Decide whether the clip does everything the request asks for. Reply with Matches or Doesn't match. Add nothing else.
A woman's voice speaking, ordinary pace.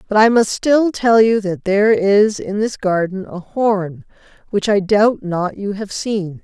Matches